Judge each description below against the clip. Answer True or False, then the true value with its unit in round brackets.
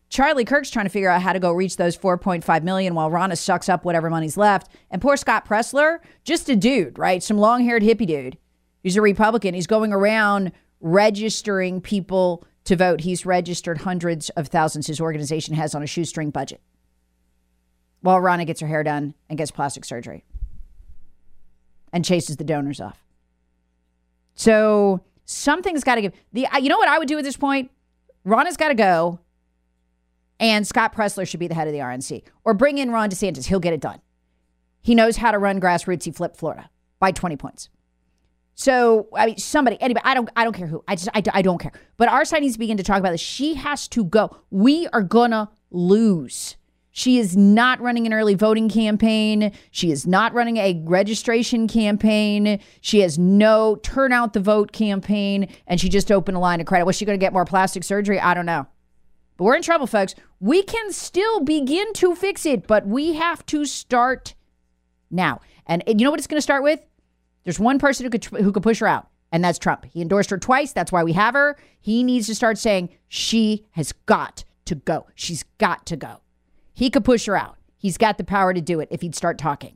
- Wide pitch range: True (5.8 semitones)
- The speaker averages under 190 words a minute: False (205 wpm)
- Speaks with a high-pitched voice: True (195 Hz)